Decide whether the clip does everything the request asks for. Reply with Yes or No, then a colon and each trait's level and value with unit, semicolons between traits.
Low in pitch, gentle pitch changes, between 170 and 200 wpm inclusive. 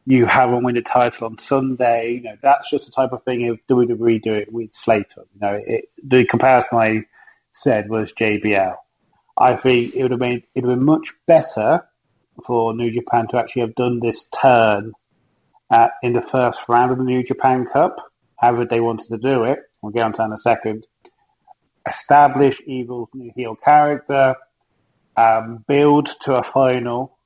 Yes: low, 120 Hz; narrow, 2.3 semitones; average, 190 wpm